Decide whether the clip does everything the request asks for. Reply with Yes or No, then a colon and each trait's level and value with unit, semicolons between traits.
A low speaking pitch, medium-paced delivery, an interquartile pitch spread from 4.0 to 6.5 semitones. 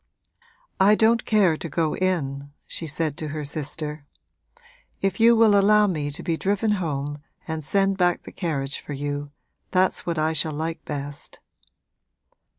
No: medium, 160 Hz; average, 155 wpm; average, 4.9 semitones